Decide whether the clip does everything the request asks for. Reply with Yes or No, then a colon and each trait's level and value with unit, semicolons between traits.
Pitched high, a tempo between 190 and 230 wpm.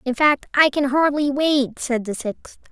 Yes: very high, 275 Hz; average, 200 wpm